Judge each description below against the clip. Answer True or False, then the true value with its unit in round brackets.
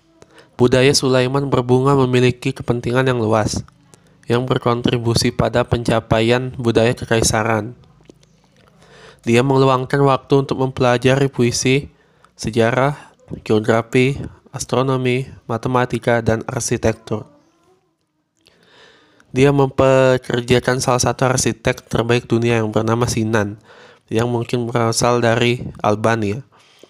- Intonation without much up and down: True (2.2 semitones)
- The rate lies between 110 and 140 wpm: False (90 wpm)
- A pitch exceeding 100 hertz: True (125 Hz)